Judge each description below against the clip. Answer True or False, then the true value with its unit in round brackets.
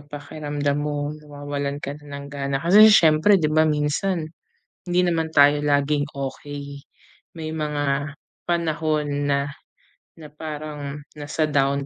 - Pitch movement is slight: True (1.6 semitones)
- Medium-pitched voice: True (150 Hz)